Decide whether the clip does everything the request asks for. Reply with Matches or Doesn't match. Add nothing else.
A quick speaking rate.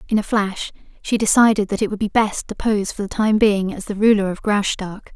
Matches